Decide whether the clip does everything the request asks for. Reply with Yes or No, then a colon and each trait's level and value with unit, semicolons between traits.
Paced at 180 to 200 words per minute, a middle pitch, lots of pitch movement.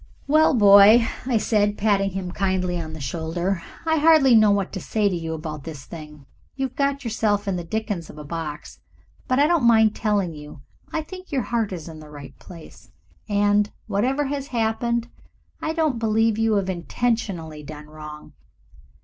No: average, 185 wpm; high, 205 Hz; wide, 6.2 semitones